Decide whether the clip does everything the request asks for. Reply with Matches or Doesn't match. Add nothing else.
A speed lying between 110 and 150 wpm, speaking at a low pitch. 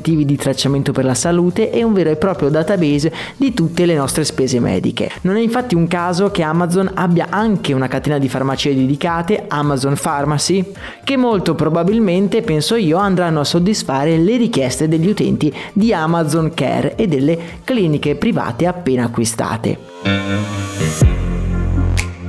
Doesn't match